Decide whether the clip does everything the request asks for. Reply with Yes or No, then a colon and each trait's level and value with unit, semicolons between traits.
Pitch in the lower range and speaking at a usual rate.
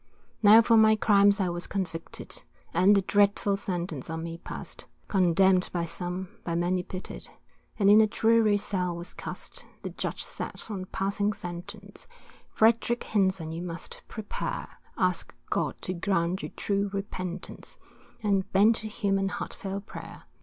No: high, 195 Hz; average, 155 wpm